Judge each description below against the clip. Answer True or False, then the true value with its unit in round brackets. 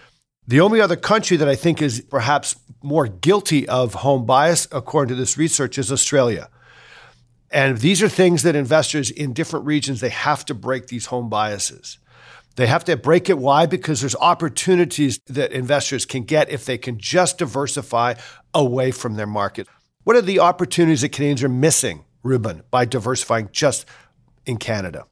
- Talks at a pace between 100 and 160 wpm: False (170 wpm)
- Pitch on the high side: False (140 Hz)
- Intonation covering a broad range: False (4.2 semitones)